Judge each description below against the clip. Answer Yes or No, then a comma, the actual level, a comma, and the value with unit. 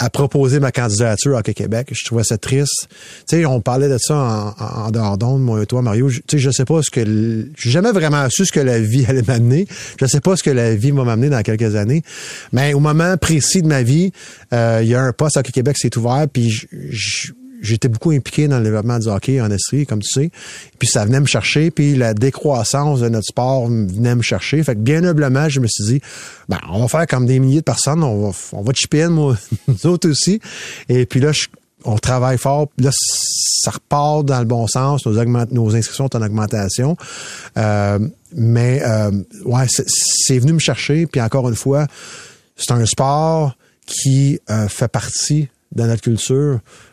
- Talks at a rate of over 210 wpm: Yes, fast, 220 wpm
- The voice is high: No, low, 130 Hz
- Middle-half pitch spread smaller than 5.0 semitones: Yes, average, 3.9 semitones